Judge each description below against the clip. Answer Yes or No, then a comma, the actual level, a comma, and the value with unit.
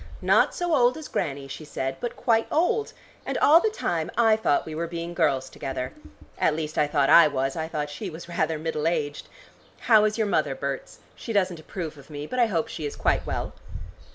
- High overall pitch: No, medium, 160 Hz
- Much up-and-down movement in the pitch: Yes, wide, 6.9 semitones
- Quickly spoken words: Yes, fast, 215 wpm